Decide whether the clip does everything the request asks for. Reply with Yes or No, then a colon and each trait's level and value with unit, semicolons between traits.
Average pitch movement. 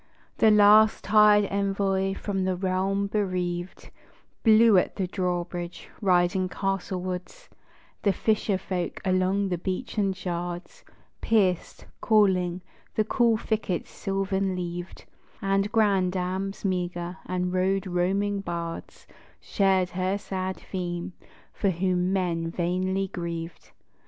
No: narrow, 1.8 semitones